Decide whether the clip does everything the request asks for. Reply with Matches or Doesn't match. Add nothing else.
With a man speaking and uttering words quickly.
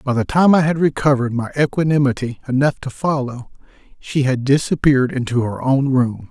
Doesn't match